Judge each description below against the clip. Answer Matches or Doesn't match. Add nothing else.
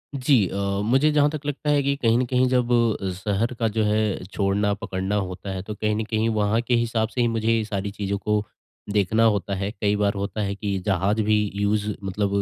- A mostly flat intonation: Matches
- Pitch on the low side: Matches